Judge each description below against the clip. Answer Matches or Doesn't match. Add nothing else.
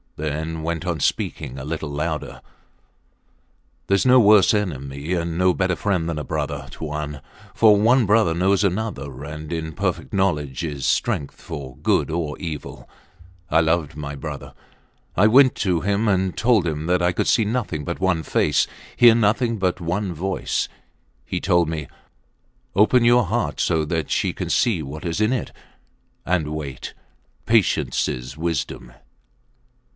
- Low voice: Matches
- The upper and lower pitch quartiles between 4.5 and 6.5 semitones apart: Matches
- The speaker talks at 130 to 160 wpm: Matches